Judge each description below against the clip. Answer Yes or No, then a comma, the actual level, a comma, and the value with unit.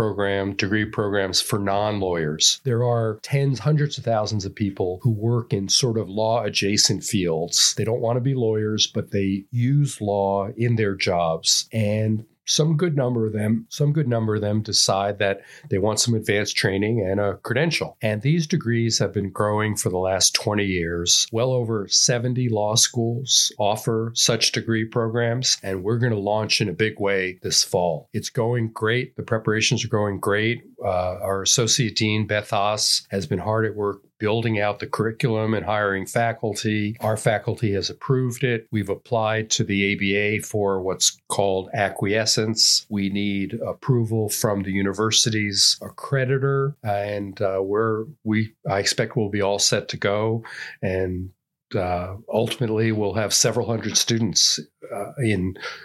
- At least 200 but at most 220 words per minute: No, average, 165 wpm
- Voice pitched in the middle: No, low, 110 Hz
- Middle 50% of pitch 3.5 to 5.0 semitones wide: No, narrow, 2.5 semitones